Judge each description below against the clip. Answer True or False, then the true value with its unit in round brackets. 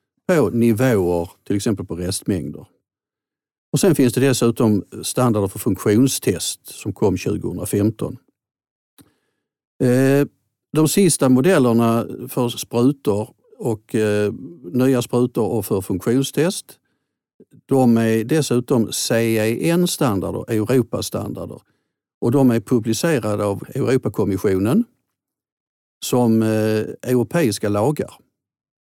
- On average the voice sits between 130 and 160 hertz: False (120 Hz)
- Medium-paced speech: False (85 wpm)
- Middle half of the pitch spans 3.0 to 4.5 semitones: True (3.8 semitones)